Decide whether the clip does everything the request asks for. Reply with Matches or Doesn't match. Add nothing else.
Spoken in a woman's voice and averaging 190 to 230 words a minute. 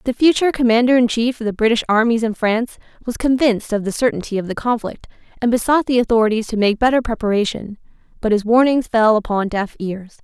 Matches